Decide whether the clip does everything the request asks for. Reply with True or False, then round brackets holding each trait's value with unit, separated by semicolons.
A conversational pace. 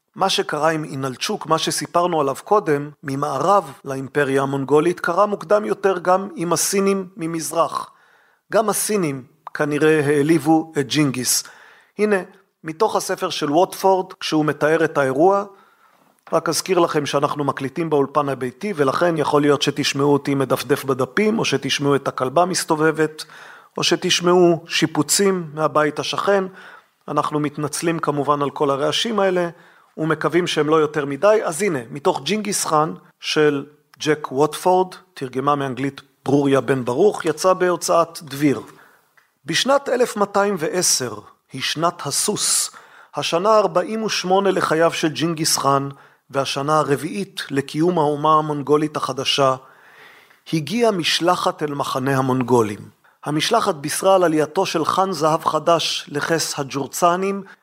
True (120 wpm)